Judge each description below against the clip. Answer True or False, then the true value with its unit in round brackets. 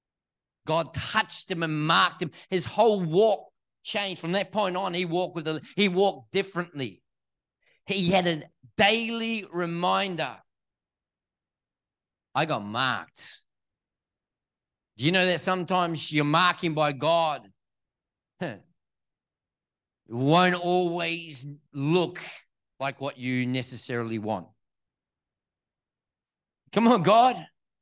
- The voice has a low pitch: False (170 Hz)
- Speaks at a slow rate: True (110 wpm)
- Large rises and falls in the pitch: True (5.7 semitones)